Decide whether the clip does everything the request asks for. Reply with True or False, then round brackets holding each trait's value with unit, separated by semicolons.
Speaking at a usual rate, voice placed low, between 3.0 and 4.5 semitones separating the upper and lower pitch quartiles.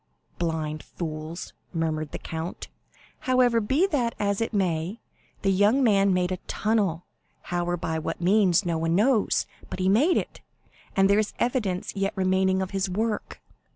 False (170 wpm; 190 Hz; 3.8 semitones)